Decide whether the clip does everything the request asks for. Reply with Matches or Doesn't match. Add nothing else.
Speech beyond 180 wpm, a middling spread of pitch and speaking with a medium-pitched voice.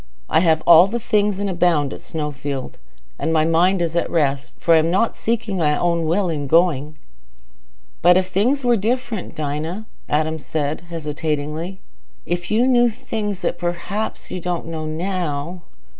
Doesn't match